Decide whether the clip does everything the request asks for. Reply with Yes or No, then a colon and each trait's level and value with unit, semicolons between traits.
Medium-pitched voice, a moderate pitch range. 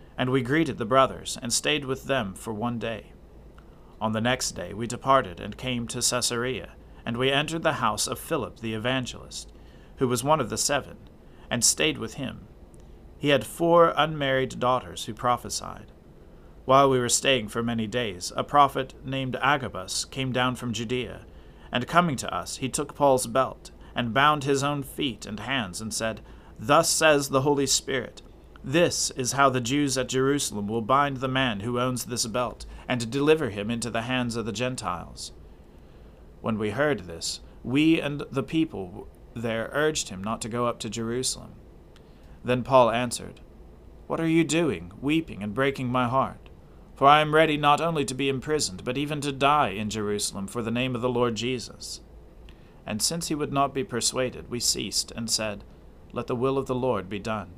No: low, 125 Hz; average, 4.2 semitones